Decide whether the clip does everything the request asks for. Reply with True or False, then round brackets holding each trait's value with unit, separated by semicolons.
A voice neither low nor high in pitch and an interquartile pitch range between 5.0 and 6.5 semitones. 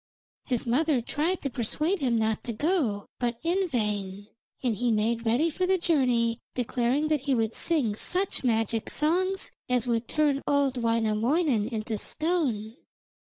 False (245 Hz; 5.3 semitones)